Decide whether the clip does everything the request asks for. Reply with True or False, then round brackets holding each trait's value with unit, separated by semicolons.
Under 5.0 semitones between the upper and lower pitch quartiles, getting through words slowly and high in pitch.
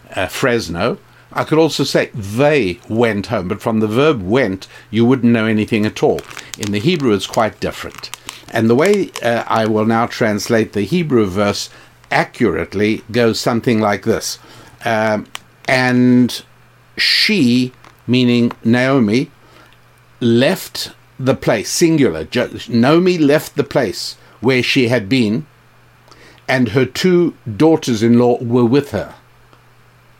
False (3.0 semitones; 130 wpm; 120 Hz)